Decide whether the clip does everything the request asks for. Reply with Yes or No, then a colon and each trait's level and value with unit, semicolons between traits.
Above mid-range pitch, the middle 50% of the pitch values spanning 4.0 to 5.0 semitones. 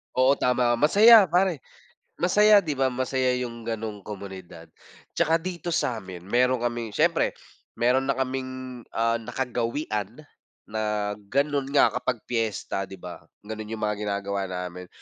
No: low, 120 Hz; average, 4.3 semitones